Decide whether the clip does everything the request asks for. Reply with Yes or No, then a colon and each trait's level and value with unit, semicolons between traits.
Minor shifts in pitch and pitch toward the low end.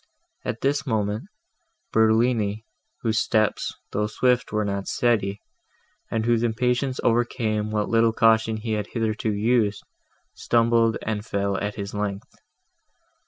Yes: narrow, 1.9 semitones; low, 110 Hz